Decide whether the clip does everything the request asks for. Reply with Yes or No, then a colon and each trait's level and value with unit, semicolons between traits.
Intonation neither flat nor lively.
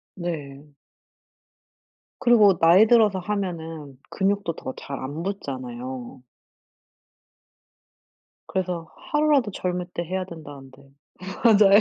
No: wide, 6.1 semitones